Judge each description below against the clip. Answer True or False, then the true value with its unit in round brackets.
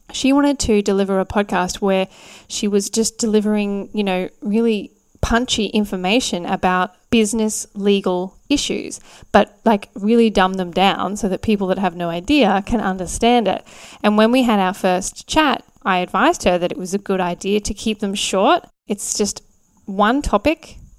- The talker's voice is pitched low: False (205 Hz)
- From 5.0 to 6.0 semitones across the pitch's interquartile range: False (3.1 semitones)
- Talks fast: False (170 wpm)